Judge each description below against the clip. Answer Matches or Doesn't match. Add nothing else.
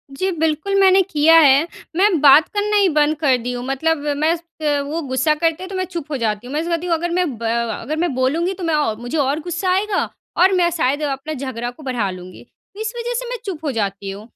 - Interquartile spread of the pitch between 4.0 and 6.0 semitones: Matches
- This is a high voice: Matches